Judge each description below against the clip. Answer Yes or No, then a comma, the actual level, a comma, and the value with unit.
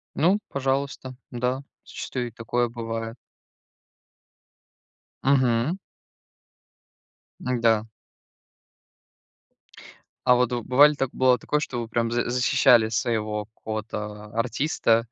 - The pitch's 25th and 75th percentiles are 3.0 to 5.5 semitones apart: No, narrow, 2.4 semitones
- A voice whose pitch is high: No, low, 120 Hz